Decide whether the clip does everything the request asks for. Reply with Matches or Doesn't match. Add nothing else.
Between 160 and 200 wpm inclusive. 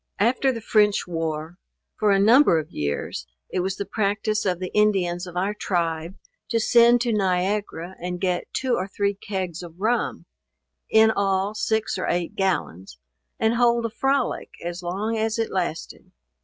Matches